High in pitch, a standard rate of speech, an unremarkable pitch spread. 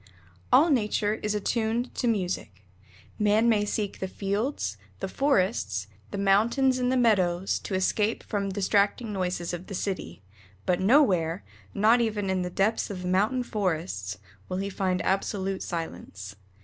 Yes: high, 200 Hz; average, 150 wpm; average, 3.2 semitones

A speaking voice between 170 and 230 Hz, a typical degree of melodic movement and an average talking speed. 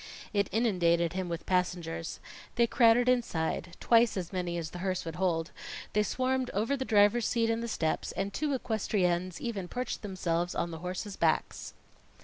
Yes: high, 190 Hz; average, 4.9 semitones; average, 170 wpm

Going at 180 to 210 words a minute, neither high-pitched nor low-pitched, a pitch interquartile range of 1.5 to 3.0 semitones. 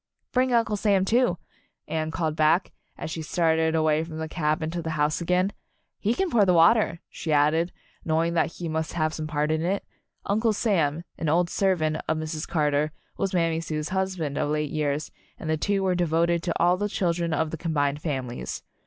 Yes: average, 195 wpm; medium, 165 Hz; narrow, 2.6 semitones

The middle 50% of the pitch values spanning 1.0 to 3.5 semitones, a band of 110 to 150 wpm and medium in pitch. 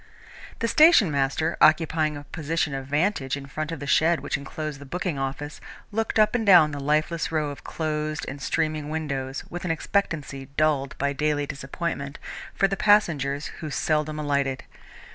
No: narrow, 2.6 semitones; average, 170 wpm; medium, 150 Hz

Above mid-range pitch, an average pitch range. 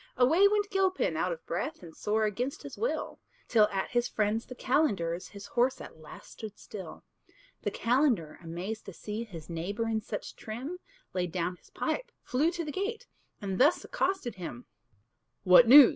No: high, 225 Hz; wide, 7.6 semitones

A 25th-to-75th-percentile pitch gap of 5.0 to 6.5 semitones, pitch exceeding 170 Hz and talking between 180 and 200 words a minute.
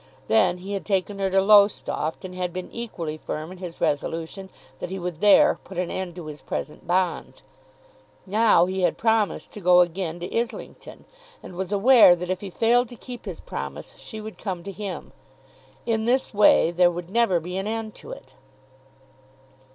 No: average, 3.2 semitones; high, 190 Hz; average, 190 wpm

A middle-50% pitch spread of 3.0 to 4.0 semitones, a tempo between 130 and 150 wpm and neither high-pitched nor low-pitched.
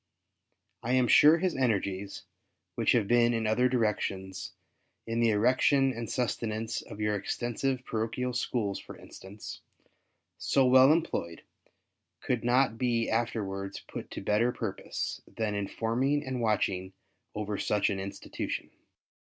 No: average, 3.4 semitones; average, 140 wpm; low, 115 Hz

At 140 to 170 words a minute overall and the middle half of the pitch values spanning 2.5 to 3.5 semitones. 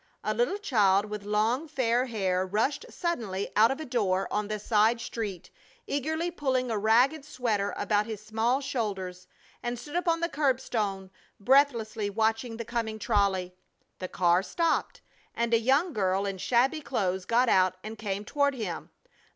No: average, 160 wpm; average, 4.8 semitones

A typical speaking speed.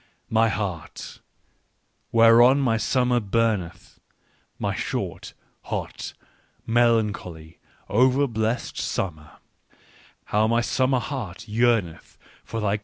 No: slow, 105 wpm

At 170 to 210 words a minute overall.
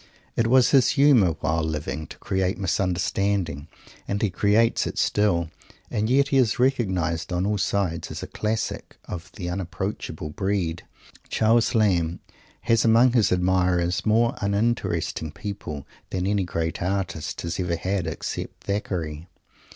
No: average, 145 wpm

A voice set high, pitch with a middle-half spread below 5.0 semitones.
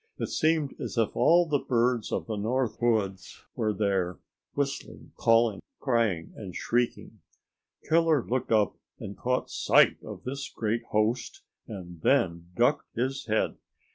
No: low, 115 Hz; average, 3.9 semitones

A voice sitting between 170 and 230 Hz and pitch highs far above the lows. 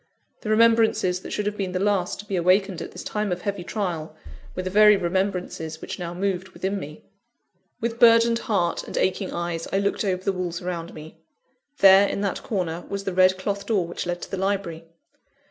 No: high, 190 Hz; narrow, 2.4 semitones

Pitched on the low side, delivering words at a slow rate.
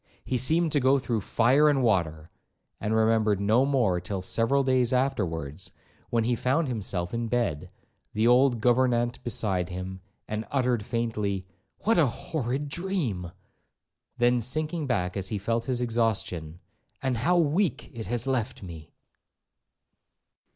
No: low, 120 Hz; average, 145 wpm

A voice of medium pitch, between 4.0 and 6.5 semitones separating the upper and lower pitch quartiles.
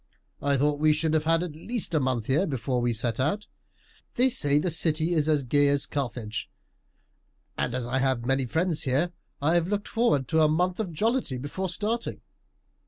Yes: medium, 150 Hz; average, 4.7 semitones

